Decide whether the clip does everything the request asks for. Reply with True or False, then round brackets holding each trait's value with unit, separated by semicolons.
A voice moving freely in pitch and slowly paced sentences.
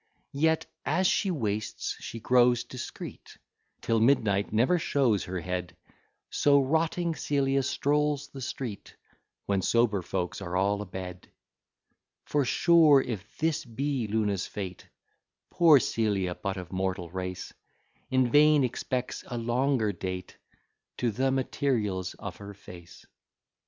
True (6.2 semitones; 130 wpm)